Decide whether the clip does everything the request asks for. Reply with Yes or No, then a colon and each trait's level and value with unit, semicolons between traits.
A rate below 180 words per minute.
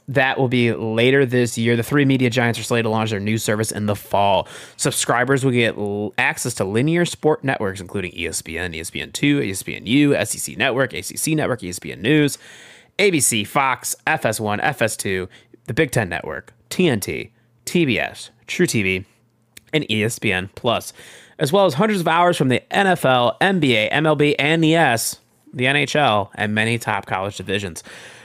Yes: average, 170 wpm